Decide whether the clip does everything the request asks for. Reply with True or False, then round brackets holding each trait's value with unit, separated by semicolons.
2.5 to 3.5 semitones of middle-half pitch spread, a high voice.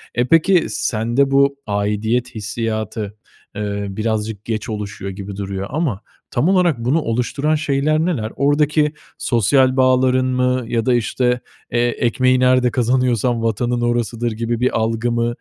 False (2.8 semitones; 120 Hz)